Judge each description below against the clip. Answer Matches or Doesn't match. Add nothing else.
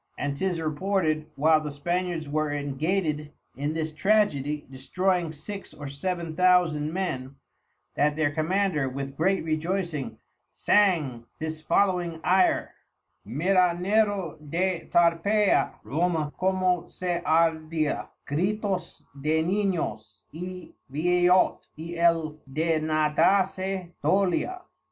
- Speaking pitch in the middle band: Matches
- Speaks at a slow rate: Matches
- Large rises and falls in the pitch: Doesn't match